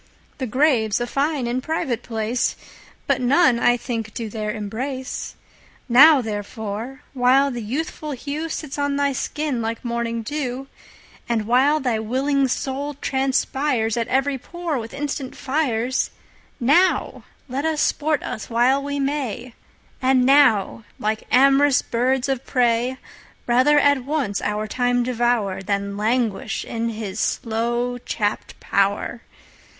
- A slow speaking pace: Yes, slow, 115 wpm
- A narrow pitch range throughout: No, average, 3.5 semitones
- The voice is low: No, very high, 250 Hz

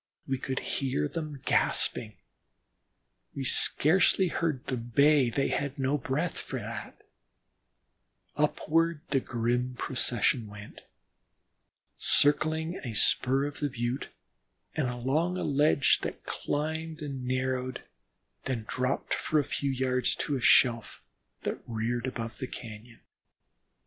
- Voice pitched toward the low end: Yes, low, 130 Hz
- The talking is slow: Yes, slow, 125 wpm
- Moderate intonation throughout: Yes, average, 3.3 semitones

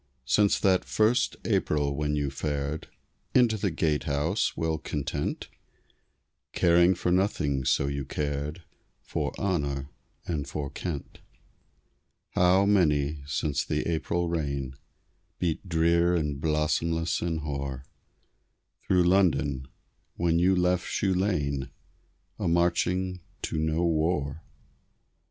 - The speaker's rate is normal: No, slow, 110 wpm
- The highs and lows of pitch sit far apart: No, average, 3.7 semitones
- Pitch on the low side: Yes, very low, 80 Hz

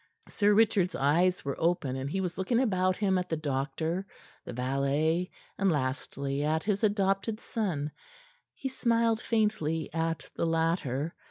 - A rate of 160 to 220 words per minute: No, average, 150 wpm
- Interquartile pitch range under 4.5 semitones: No, average, 5.2 semitones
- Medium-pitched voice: Yes, medium, 170 Hz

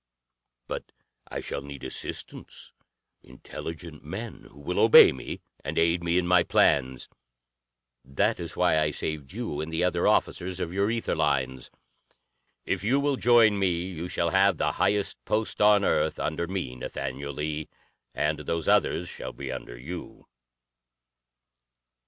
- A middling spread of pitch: Yes, average, 5.0 semitones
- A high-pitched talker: No, very low, 85 Hz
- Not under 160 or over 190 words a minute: No, average, 150 wpm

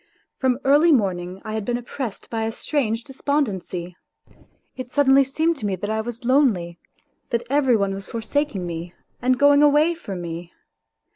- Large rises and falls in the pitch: Yes, wide, 6.4 semitones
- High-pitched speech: Yes, high, 235 Hz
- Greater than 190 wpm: No, average, 165 wpm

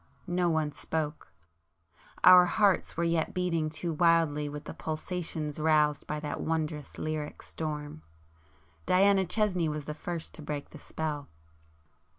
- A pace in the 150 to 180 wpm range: No, slow, 135 wpm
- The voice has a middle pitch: Yes, medium, 155 Hz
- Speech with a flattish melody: Yes, narrow, 2.2 semitones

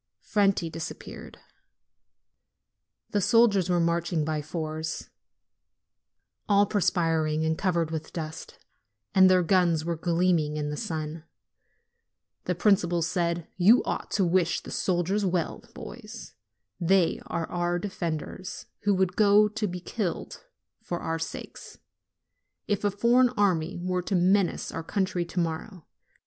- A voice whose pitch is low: No, medium, 175 Hz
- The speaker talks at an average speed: No, slow, 130 wpm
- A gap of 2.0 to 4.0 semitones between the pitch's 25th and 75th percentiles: Yes, average, 3.2 semitones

